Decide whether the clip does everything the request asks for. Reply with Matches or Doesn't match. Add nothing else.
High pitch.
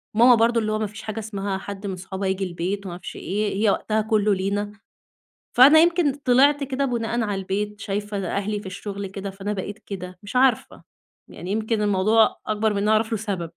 Matches